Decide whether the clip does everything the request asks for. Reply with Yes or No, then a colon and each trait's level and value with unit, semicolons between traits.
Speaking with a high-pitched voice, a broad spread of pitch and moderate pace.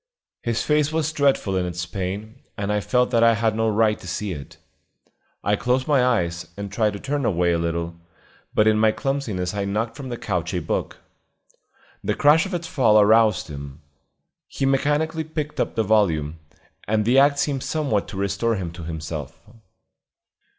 No: low, 110 Hz; wide, 6.8 semitones; average, 185 wpm